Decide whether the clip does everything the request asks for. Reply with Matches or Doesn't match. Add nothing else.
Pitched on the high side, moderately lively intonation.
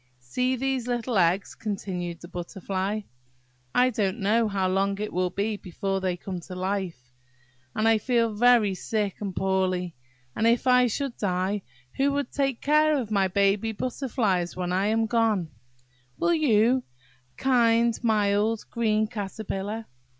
Matches